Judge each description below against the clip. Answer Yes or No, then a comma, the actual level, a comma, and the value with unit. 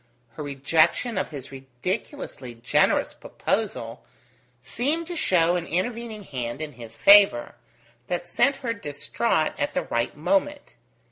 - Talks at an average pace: No, slow, 130 wpm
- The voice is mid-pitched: Yes, medium, 170 Hz